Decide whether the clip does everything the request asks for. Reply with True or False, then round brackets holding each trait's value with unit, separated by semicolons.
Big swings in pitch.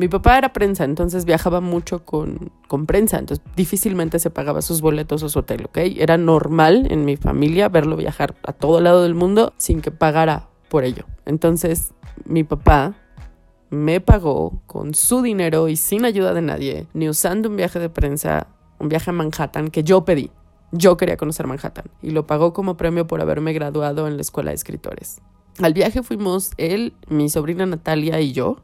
False (2.9 semitones)